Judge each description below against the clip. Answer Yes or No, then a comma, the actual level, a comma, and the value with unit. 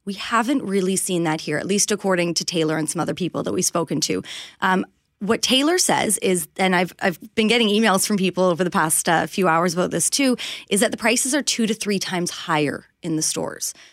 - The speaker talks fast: Yes, fast, 235 wpm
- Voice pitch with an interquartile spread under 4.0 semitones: No, average, 4.7 semitones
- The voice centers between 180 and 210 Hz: Yes, medium, 185 Hz